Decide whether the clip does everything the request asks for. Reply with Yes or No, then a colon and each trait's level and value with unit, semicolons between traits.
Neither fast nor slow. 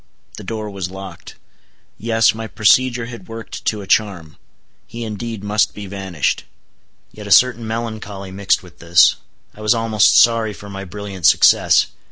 Yes: average, 160 wpm